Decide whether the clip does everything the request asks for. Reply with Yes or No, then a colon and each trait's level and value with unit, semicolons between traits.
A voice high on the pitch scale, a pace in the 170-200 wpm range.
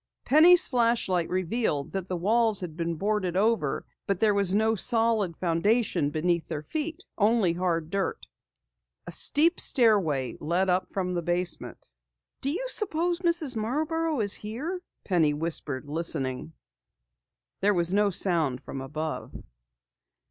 No: high, 195 Hz; average, 140 wpm